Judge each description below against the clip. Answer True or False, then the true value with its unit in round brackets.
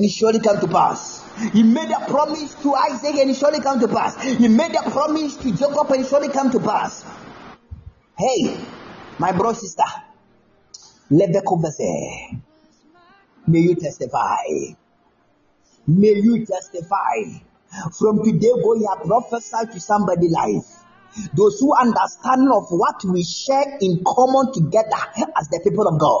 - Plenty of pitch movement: True (5.7 semitones)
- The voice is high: True (225 Hz)